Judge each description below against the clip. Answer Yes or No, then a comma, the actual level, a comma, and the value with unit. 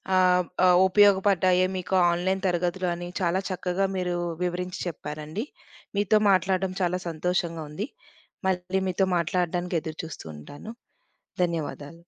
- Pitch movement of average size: No, narrow, 1.6 semitones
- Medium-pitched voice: Yes, medium, 180 Hz